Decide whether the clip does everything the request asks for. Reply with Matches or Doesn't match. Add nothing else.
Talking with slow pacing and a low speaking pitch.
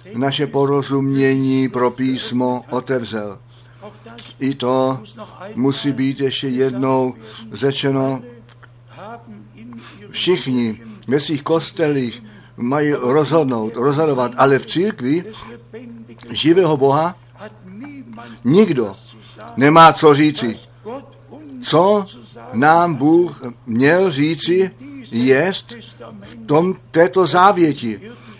Matches